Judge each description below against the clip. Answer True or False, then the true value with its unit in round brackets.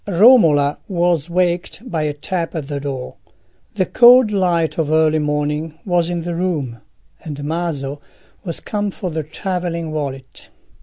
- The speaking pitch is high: False (165 Hz)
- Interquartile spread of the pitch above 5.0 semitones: False (3.4 semitones)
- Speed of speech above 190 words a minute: False (150 wpm)